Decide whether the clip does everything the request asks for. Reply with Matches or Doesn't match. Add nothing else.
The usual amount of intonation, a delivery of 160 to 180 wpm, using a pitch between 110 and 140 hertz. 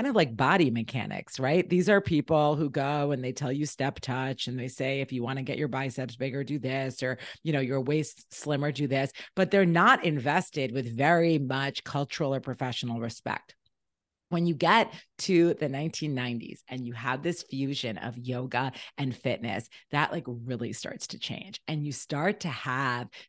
Doesn't match